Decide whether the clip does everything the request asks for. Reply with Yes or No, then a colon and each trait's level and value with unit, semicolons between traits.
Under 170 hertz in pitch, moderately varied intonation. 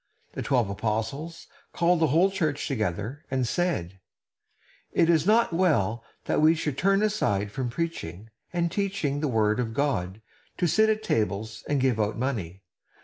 No: low, 135 Hz; wide, 7.6 semitones